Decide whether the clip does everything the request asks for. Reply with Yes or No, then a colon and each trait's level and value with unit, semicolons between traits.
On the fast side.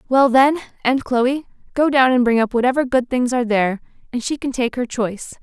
Yes: fast, 220 wpm